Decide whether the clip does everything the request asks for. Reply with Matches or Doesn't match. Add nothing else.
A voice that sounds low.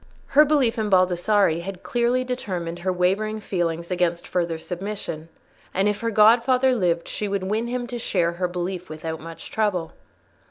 Doesn't match